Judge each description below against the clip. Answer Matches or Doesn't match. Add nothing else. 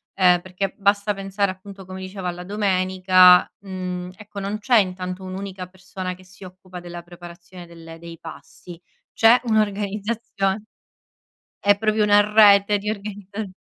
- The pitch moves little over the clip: Matches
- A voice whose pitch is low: Doesn't match